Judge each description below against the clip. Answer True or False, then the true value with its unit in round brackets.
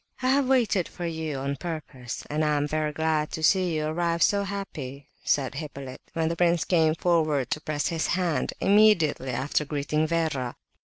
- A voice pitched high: False (155 Hz)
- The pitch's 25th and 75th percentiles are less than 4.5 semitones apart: True (2.9 semitones)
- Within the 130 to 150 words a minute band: False (175 wpm)